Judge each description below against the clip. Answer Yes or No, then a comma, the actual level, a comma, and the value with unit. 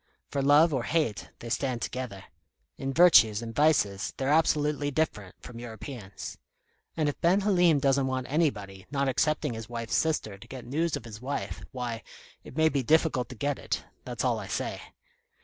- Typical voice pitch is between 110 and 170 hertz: Yes, low, 135 Hz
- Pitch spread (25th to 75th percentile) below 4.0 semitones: No, average, 4.8 semitones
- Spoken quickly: No, average, 180 wpm